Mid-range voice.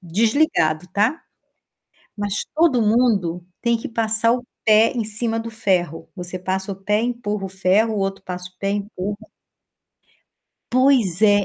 No: high, 210 Hz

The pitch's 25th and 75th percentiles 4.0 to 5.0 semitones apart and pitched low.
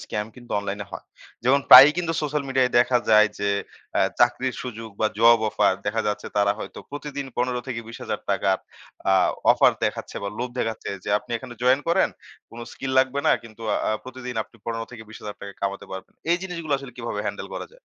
No: average, 3.3 semitones; low, 125 Hz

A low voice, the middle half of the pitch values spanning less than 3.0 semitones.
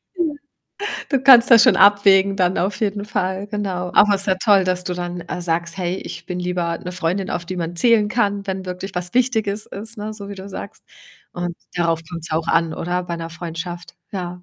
No: medium, 185 Hz; narrow, 2.6 semitones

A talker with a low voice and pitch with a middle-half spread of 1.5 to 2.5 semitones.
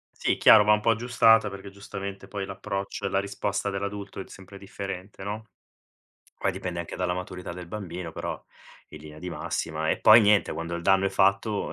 Yes: low, 100 Hz; narrow, 2.0 semitones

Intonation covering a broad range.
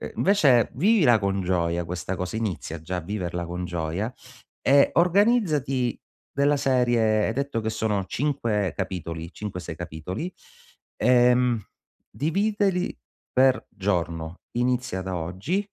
Yes: wide, 7.3 semitones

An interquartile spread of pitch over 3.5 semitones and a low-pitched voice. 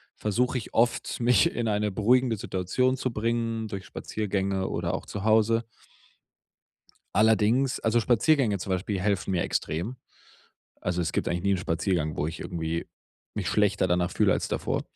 Yes: average, 4.1 semitones; low, 105 Hz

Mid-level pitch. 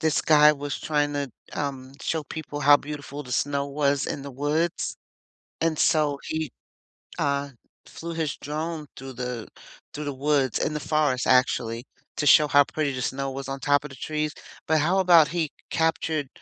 Yes: medium, 145 Hz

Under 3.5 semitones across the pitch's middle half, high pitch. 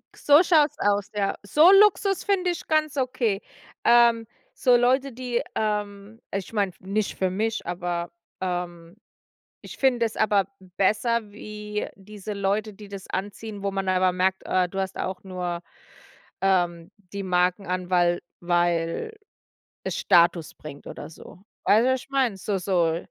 No: average, 4.2 semitones; high, 200 Hz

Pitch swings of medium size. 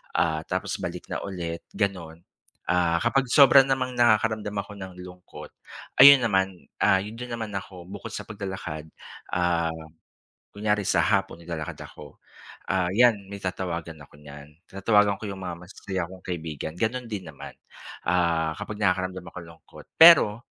Yes: average, 3.8 semitones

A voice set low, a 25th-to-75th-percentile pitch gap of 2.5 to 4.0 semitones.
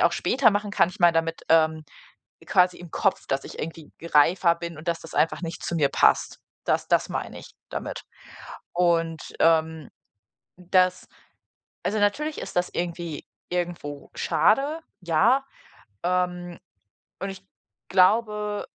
No: medium, 175 Hz; average, 2.8 semitones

